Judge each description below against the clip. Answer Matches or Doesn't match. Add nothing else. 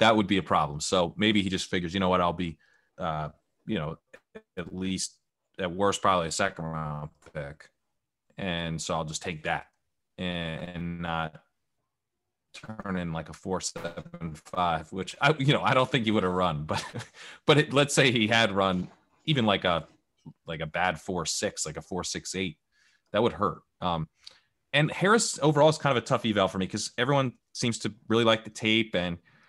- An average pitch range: Matches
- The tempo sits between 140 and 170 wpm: Doesn't match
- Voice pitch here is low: Matches